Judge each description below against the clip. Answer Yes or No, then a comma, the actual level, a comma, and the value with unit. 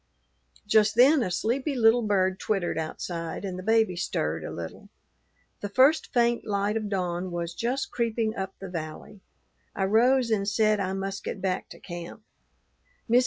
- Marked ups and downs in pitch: No, average, 3.9 semitones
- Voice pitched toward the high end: Yes, high, 200 Hz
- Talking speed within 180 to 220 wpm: No, average, 165 wpm